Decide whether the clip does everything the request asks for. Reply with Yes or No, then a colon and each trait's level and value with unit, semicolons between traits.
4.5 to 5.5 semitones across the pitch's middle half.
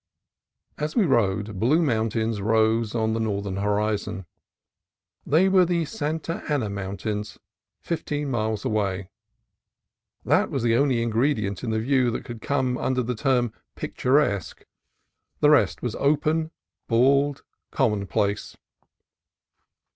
Yes: average, 5.0 semitones